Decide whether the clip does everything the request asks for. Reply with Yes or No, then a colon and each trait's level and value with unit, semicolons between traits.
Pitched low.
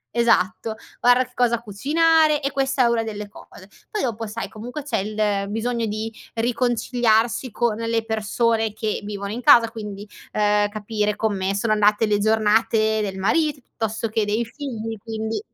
No: high, 225 Hz